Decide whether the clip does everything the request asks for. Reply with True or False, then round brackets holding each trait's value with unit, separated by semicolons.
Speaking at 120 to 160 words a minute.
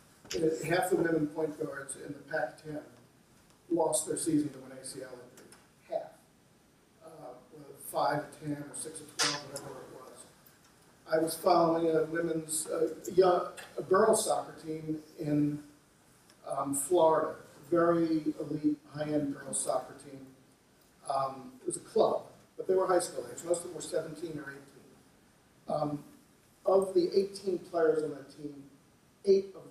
True (155 wpm)